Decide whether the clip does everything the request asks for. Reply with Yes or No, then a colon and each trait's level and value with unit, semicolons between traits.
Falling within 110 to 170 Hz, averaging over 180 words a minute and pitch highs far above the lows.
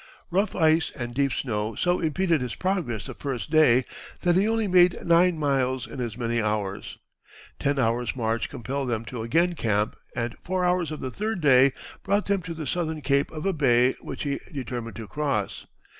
Yes: medium, 140 Hz; average, 190 wpm; wide, 6.3 semitones